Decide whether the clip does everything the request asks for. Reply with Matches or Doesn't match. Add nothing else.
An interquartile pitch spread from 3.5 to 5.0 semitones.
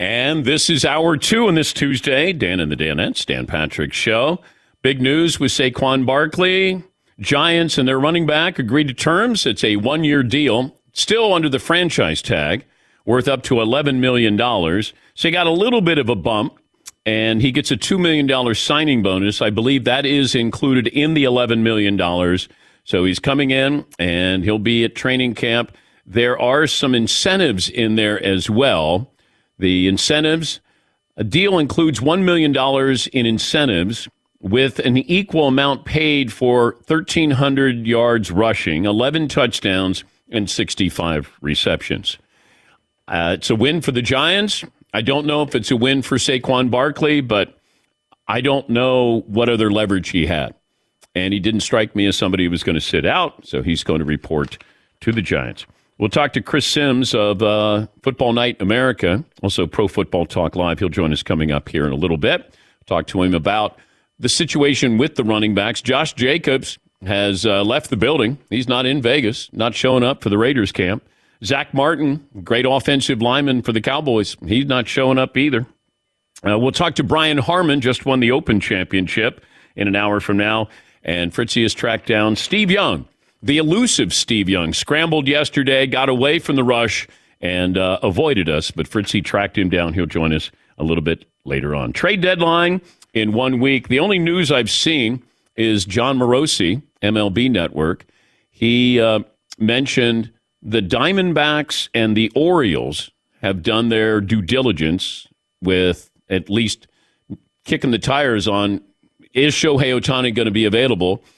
Doesn't match